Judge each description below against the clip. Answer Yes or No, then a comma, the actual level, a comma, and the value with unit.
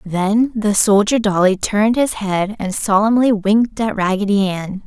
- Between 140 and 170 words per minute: Yes, average, 160 wpm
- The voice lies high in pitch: Yes, high, 205 Hz